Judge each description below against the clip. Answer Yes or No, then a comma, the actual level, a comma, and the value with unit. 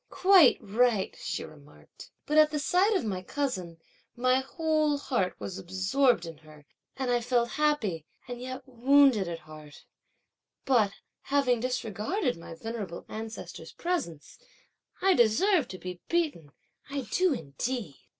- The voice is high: Yes, high, 240 Hz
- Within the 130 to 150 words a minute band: Yes, average, 140 wpm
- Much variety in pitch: Yes, wide, 7.4 semitones